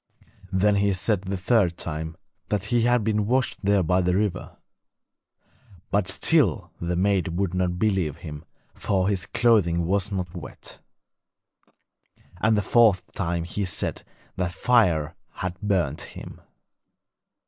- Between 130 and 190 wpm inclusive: Yes, slow, 135 wpm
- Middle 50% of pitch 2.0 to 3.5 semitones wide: Yes, average, 3.0 semitones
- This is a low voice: Yes, very low, 95 Hz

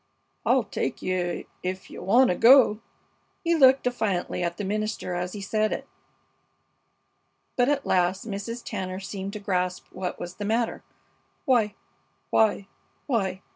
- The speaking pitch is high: Yes, high, 205 Hz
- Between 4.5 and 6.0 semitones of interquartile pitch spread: No, average, 3.8 semitones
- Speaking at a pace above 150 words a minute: No, average, 140 wpm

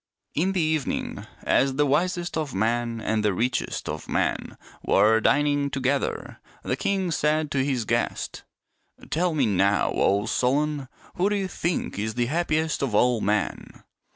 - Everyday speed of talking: Yes, average, 160 wpm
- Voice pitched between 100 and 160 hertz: Yes, medium, 140 Hz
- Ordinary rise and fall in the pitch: No, wide, 5.7 semitones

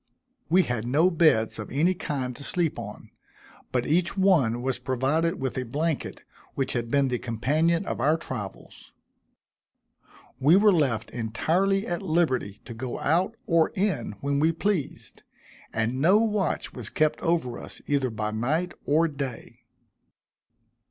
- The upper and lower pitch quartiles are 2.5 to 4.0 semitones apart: No, wide, 5.5 semitones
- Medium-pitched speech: Yes, medium, 145 Hz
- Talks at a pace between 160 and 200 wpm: No, average, 150 wpm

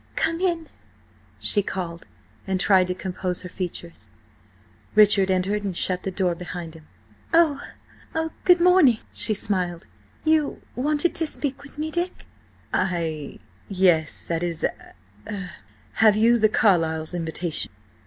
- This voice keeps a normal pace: No, slow, 110 wpm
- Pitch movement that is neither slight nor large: No, wide, 8.3 semitones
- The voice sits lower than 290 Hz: Yes, high, 190 Hz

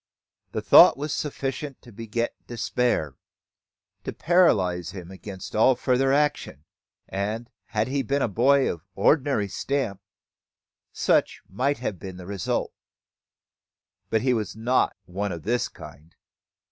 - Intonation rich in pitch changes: Yes, wide, 5.7 semitones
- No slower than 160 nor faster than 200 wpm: No, slow, 135 wpm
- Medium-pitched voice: No, low, 115 Hz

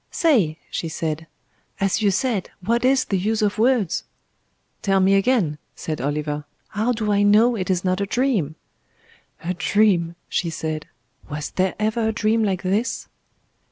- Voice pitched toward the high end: Yes, high, 195 Hz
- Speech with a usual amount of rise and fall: Yes, average, 4.7 semitones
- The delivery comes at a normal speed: Yes, average, 160 wpm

